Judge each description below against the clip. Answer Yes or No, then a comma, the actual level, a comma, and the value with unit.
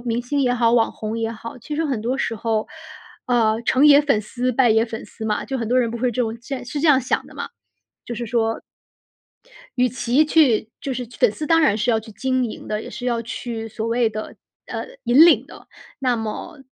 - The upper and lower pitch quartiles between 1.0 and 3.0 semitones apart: Yes, narrow, 2.5 semitones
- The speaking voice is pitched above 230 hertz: Yes, high, 240 Hz